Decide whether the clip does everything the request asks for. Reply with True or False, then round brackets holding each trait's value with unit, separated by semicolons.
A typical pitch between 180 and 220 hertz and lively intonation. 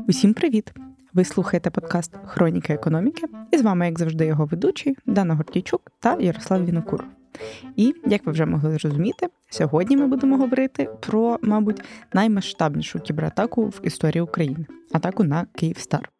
True (190 Hz; 6.1 semitones)